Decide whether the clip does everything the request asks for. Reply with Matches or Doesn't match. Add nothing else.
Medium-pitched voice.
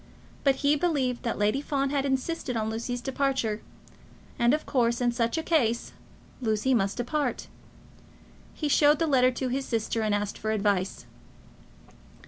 Doesn't match